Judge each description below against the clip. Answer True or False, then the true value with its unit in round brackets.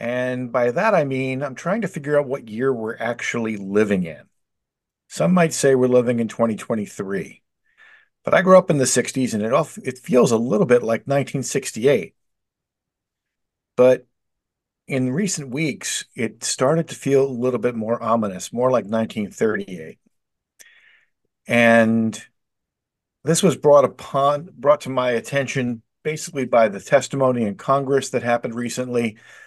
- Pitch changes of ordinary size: True (3.7 semitones)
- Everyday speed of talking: True (150 wpm)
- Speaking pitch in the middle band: False (125 Hz)